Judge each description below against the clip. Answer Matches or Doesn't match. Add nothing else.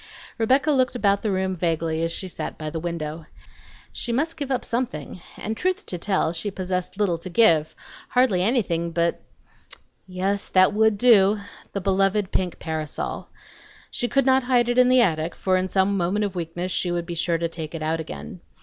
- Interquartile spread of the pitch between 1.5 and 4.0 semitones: Doesn't match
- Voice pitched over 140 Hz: Matches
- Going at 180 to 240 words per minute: Matches